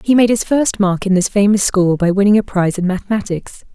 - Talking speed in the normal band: No, fast, 240 wpm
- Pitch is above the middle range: Yes, high, 200 Hz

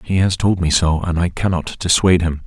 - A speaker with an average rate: No, fast, 245 wpm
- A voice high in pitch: No, very low, 85 Hz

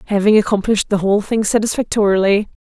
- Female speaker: Yes, female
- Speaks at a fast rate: No, slow, 135 wpm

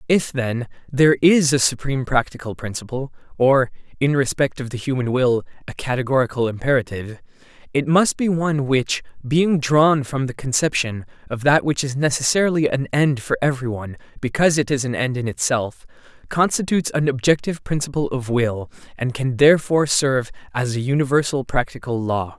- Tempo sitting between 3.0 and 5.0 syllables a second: No, 5.6 syllables/s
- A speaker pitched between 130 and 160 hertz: Yes, low, 135 Hz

